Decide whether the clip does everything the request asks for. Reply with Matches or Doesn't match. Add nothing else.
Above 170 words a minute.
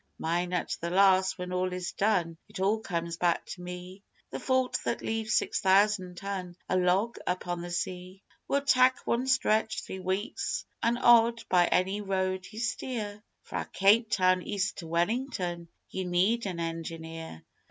Doesn't match